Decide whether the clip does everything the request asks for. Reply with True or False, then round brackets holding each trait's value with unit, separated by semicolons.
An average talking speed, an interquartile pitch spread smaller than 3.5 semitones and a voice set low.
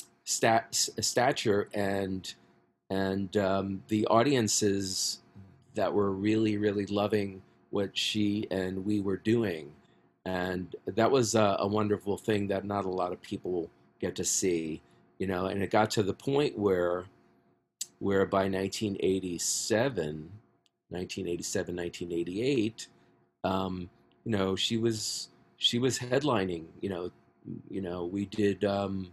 False (130 wpm; 2.7 semitones; 95 Hz)